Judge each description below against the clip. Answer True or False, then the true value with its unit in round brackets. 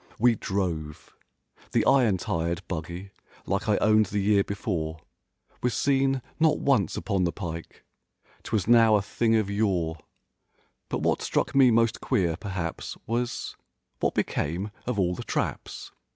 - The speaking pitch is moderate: False (100 Hz)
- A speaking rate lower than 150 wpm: True (140 wpm)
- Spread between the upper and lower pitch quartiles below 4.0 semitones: False (4.9 semitones)